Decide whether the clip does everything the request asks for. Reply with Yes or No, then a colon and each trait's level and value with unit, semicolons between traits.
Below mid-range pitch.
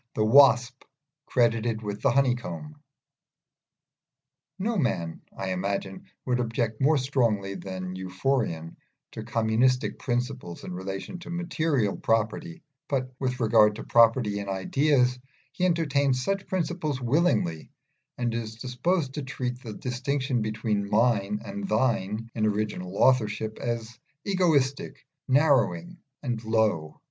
Yes: low, 120 Hz